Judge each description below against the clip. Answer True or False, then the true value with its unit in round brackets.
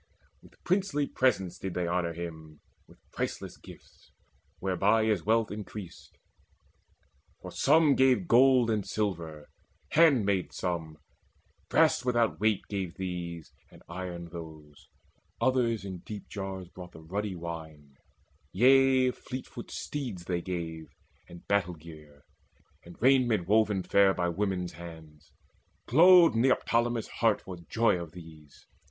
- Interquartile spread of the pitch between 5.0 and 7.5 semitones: True (5.4 semitones)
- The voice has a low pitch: True (95 Hz)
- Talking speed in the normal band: False (125 wpm)